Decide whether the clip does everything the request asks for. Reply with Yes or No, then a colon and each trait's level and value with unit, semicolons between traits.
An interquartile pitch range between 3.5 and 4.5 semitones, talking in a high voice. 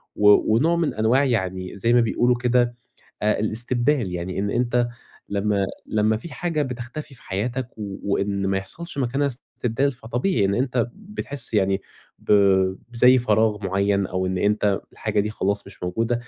No: average, 3.8 semitones; low, 110 Hz